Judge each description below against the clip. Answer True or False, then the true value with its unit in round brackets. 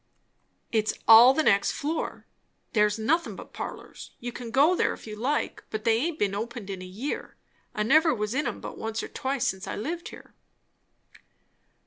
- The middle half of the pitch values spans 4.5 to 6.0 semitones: True (5.1 semitones)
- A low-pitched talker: False (230 Hz)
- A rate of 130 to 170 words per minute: False (185 wpm)